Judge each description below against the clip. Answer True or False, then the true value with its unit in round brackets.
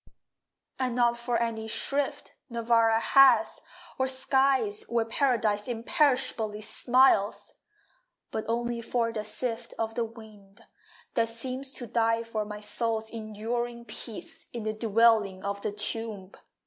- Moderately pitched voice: False (230 Hz)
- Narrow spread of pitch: True (1.9 semitones)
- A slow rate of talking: True (130 wpm)